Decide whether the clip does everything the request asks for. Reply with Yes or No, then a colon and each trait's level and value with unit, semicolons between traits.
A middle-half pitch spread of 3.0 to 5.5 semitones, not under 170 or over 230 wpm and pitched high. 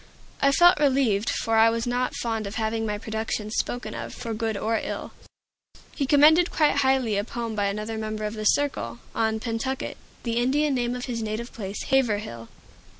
Yes: average, 3.3 semitones; average, 185 wpm; high, 225 Hz